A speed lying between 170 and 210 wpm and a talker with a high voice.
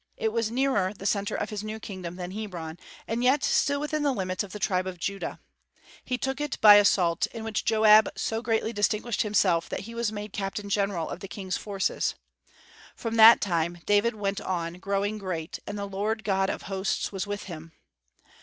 Yes: average, 200 wpm; high, 205 Hz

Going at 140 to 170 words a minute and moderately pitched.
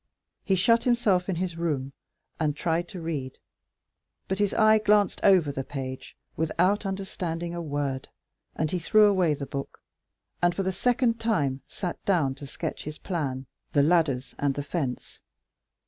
Yes: average, 165 wpm; medium, 170 Hz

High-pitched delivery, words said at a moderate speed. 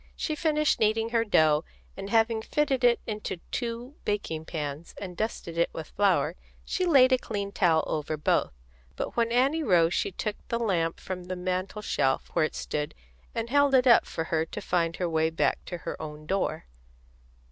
Yes: high, 195 Hz; average, 190 wpm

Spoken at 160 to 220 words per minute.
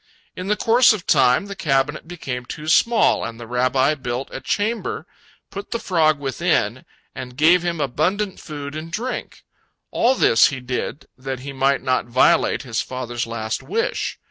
Yes: average, 170 wpm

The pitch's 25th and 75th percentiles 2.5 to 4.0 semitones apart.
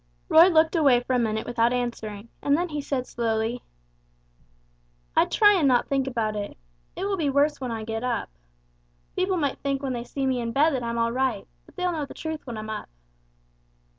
No: average, 4.4 semitones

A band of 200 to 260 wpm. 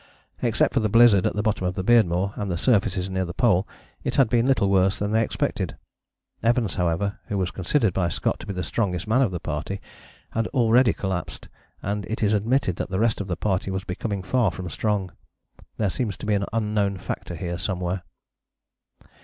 Yes: fast, 205 wpm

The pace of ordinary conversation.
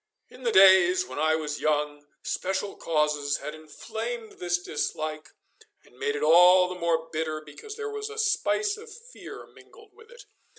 Yes: average, 170 wpm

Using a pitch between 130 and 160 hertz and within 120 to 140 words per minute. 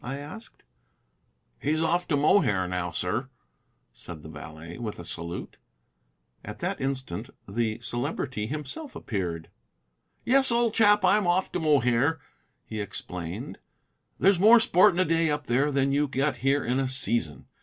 No: low, 135 Hz; average, 155 wpm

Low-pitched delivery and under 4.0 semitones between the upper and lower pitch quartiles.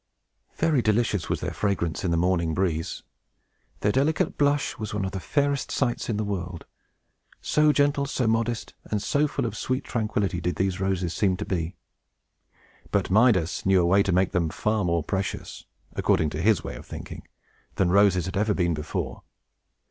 No: low, 100 Hz; average, 4.3 semitones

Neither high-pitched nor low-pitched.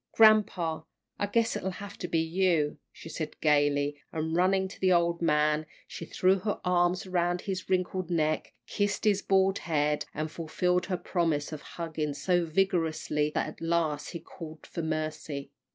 Yes: medium, 170 Hz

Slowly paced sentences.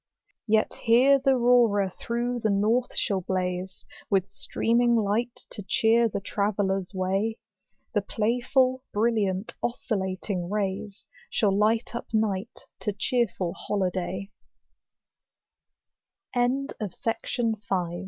Yes: slow, 95 wpm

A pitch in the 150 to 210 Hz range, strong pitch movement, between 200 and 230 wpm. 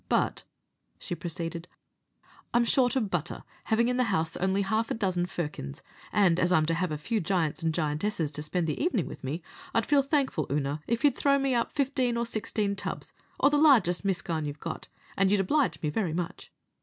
Yes: high, 190 Hz; wide, 6.4 semitones; fast, 205 wpm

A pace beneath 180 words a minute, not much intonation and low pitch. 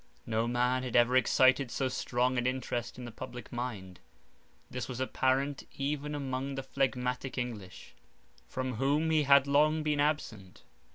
Yes: average, 155 wpm; narrow, 2.2 semitones; low, 130 Hz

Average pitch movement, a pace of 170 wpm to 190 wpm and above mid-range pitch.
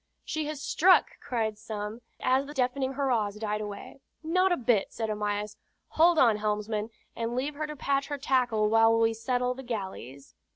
Yes: average, 4.4 semitones; average, 175 wpm; high, 235 Hz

